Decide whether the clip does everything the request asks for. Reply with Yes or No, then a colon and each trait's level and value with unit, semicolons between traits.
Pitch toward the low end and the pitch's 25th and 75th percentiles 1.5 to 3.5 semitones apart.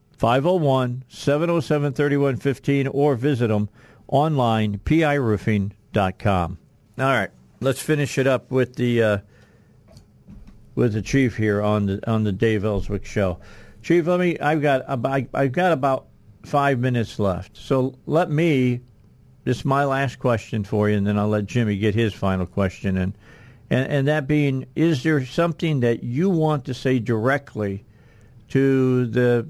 No: low, 125 Hz; average, 4.8 semitones